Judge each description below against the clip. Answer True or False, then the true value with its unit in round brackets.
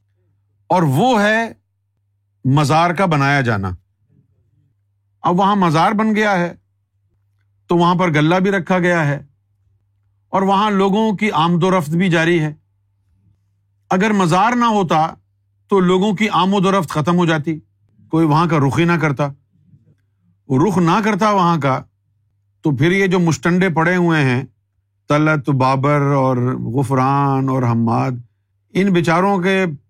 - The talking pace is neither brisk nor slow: True (150 wpm)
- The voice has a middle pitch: True (145 Hz)